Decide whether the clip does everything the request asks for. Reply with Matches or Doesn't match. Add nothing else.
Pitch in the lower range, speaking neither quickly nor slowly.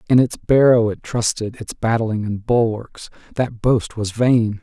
Matches